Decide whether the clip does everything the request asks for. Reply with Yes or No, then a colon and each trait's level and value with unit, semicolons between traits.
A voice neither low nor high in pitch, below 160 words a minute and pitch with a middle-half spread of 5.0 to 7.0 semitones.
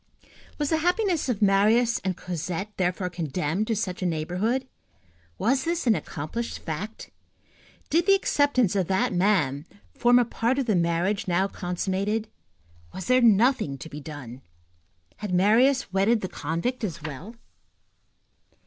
No: high, 200 Hz; average, 145 wpm; wide, 5.4 semitones